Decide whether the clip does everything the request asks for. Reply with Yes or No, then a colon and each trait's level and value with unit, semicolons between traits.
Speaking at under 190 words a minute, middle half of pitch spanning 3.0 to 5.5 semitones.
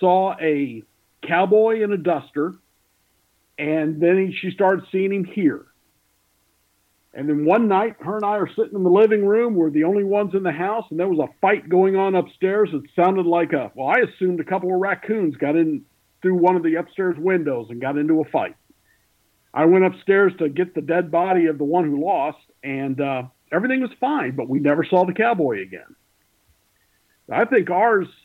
No: average, 200 wpm; average, 3.9 semitones